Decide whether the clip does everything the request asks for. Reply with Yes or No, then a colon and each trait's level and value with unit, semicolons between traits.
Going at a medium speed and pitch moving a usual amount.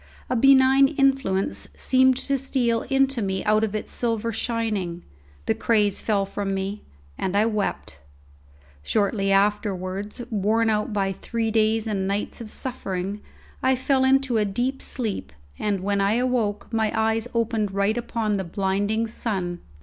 Yes: average, 150 wpm; average, 3.3 semitones